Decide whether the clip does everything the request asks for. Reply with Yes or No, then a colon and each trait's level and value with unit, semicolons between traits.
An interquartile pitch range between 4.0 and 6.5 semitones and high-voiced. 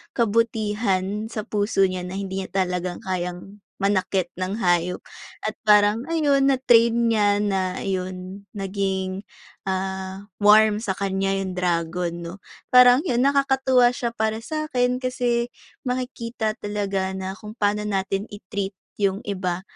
No: average, 3.5 semitones; high, 205 Hz